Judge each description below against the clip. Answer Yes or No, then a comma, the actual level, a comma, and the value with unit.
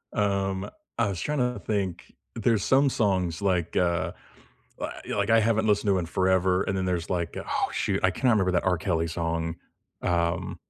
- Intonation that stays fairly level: No, average, 3.1 semitones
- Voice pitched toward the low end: Yes, very low, 95 Hz